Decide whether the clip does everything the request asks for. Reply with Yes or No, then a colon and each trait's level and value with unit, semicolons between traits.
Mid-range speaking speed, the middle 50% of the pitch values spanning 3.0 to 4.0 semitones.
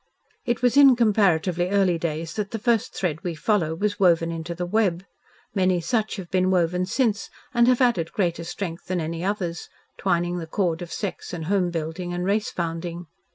Yes: average, 190 wpm; average, 3.5 semitones